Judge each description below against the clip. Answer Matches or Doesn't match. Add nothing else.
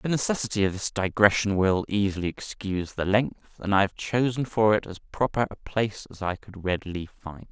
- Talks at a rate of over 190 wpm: Matches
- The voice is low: Matches